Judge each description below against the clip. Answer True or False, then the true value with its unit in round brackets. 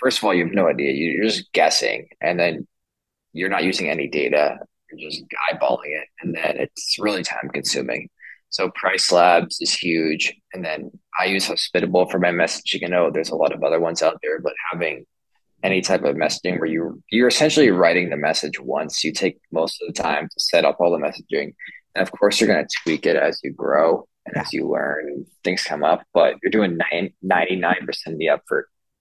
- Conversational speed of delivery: False (215 wpm)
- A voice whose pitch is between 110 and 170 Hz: False (100 Hz)